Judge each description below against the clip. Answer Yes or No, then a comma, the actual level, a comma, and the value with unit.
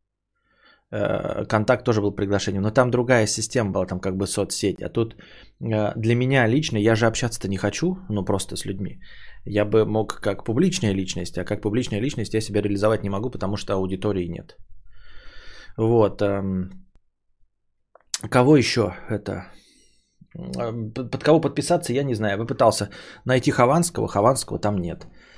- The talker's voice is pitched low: Yes, low, 105 Hz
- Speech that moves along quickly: No, average, 150 wpm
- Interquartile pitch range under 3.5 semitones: No, average, 3.8 semitones